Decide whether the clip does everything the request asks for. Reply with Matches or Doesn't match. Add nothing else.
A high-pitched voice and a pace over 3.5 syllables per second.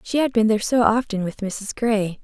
Matches